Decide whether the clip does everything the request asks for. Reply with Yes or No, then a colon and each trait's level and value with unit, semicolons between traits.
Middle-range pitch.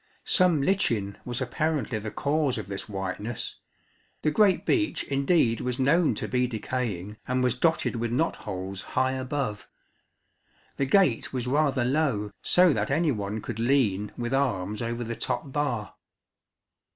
No: low, 125 Hz